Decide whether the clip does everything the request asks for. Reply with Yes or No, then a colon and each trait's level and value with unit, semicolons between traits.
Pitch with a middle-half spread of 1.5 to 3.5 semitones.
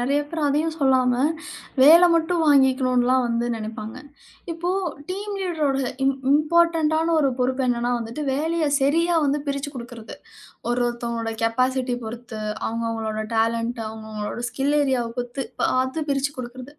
No: average, 4.1 semitones